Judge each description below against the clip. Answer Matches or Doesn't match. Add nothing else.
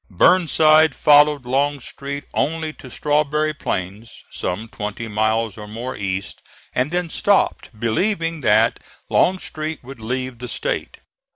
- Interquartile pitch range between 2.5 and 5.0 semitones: Doesn't match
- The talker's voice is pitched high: Doesn't match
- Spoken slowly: Matches